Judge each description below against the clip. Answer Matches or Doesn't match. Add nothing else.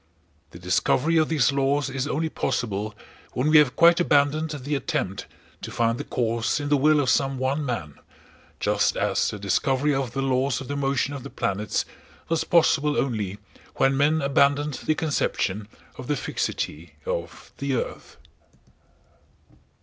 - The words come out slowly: Doesn't match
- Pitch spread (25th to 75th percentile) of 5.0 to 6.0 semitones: Doesn't match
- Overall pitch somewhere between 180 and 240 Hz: Doesn't match